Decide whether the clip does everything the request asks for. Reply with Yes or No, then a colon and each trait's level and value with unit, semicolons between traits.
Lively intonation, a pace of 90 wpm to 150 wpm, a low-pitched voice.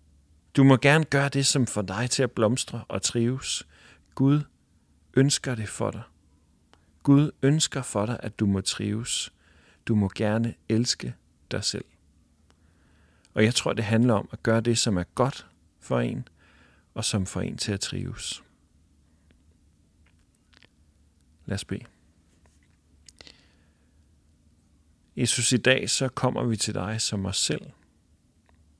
Yes: wide, 7.0 semitones; average, 140 wpm; very low, 95 Hz